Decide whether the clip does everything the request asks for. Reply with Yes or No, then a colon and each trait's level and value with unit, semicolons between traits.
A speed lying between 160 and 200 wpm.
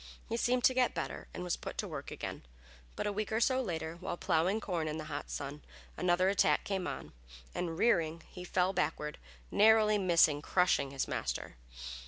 Yes: average, 190 wpm